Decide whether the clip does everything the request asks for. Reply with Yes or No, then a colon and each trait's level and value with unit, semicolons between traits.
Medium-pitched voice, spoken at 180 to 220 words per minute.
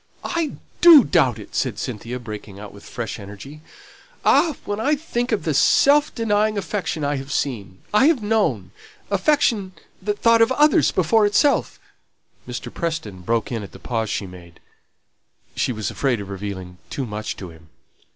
No: medium, 145 Hz; average, 170 wpm